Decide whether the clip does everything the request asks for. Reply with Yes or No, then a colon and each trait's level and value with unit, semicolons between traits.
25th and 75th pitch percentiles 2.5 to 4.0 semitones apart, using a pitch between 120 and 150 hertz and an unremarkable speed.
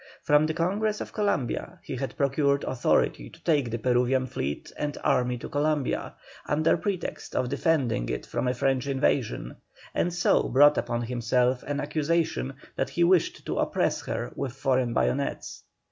Yes: average, 3.7 semitones; medium, 140 Hz; average, 160 wpm